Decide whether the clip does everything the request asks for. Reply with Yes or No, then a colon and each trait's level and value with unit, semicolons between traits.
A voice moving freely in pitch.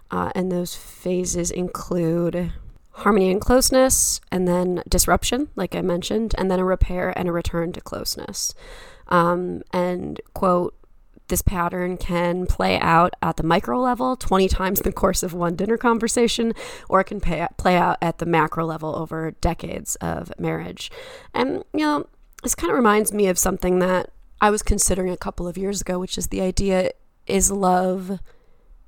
No: average, 3.0 semitones